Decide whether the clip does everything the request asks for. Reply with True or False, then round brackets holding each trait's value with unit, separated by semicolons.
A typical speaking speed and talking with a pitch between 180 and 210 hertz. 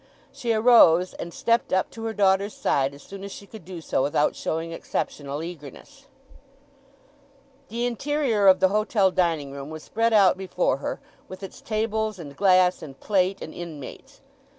True (170 wpm; 190 Hz)